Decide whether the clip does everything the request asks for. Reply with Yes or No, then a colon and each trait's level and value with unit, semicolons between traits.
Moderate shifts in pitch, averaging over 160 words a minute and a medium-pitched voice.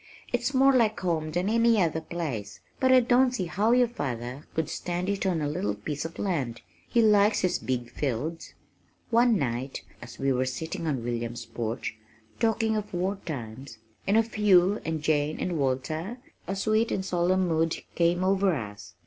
No: wide, 7.3 semitones; average, 180 wpm; medium, 170 Hz